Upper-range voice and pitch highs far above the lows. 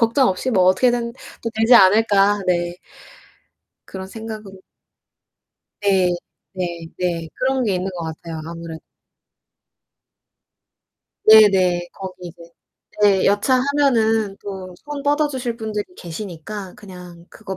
No: high, 195 Hz; average, 3.9 semitones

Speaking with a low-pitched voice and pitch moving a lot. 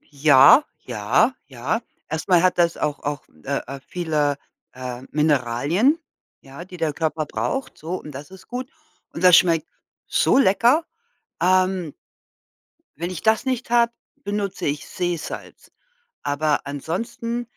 No: medium, 170 Hz; wide, 5.9 semitones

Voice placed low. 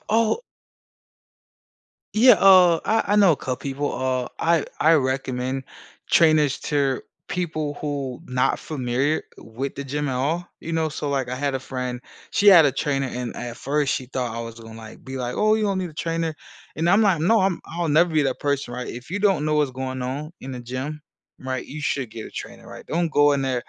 No: medium, 145 Hz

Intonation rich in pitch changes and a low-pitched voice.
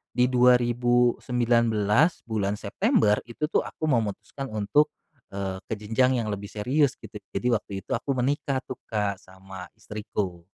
No: average, 3.6 semitones; low, 115 Hz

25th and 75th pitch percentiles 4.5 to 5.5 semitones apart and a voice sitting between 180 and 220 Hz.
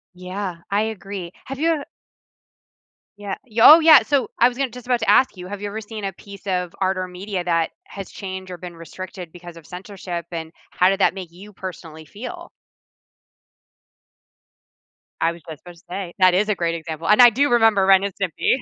No: average, 3.3 semitones; high, 190 Hz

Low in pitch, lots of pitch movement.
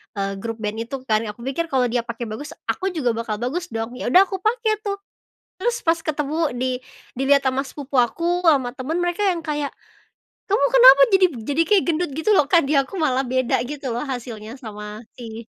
No: very high, 275 Hz; wide, 6.1 semitones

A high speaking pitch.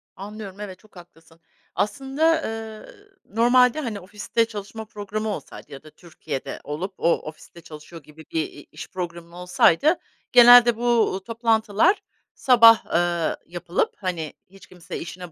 Yes: high, 200 Hz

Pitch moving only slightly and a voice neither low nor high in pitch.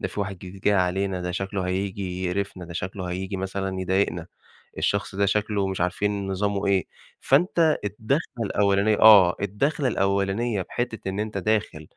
No: narrow, 1.8 semitones; low, 100 Hz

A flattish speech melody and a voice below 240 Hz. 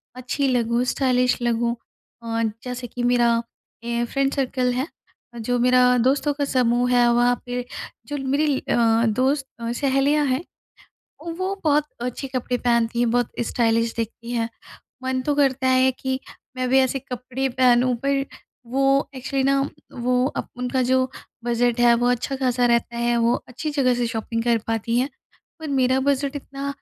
No: narrow, 2.0 semitones; very high, 250 Hz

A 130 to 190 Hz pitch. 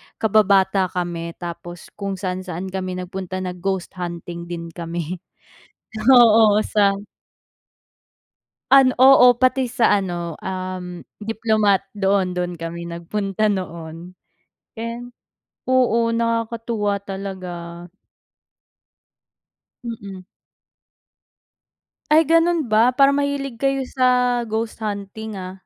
No: high, 200 Hz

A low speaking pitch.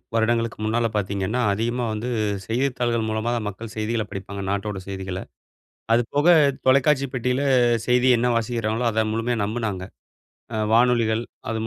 Yes: low, 115 Hz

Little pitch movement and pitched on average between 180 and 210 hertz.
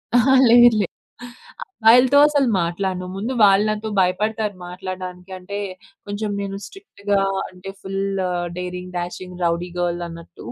No: average, 3.2 semitones; high, 195 Hz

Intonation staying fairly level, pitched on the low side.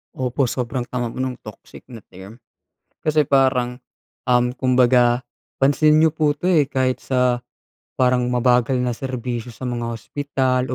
Yes: narrow, 1.7 semitones; low, 125 Hz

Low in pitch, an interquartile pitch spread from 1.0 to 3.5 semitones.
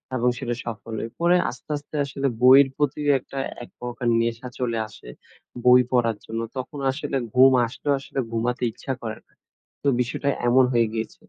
Yes: low, 125 Hz; average, 2.8 semitones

